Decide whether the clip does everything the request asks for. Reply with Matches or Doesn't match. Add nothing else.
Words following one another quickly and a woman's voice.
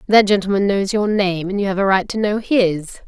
Matches